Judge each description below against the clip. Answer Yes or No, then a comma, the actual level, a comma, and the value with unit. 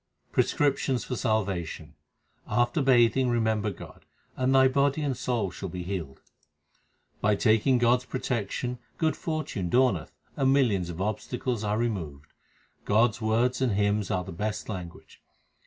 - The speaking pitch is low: Yes, low, 110 Hz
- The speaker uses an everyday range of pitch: Yes, average, 4.6 semitones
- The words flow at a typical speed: Yes, average, 145 wpm